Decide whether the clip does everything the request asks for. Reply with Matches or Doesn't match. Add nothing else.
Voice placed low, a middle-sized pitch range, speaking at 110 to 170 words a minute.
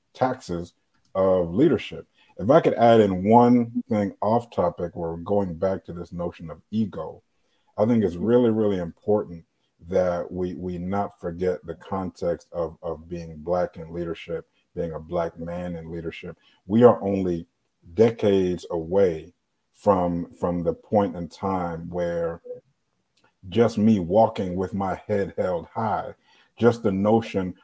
Matches